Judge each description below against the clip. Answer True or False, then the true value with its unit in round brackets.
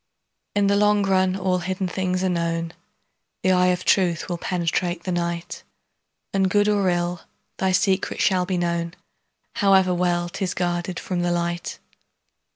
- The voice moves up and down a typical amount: False (1.5 semitones)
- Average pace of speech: True (160 wpm)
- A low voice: False (180 Hz)